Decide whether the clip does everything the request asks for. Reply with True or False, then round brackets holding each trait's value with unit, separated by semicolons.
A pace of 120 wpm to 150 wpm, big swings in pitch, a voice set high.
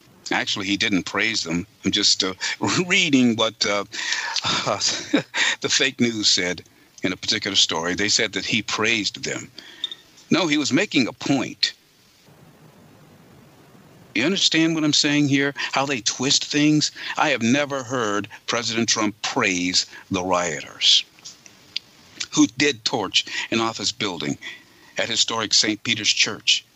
False (140 wpm; 6.2 semitones; 120 Hz)